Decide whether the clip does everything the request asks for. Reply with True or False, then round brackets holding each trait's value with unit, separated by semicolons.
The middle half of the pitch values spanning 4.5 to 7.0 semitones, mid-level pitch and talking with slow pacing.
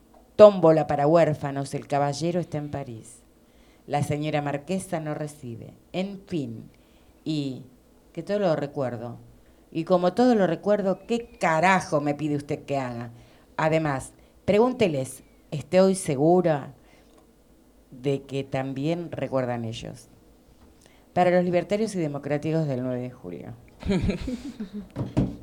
True (4.8 semitones; 150 Hz; 120 wpm)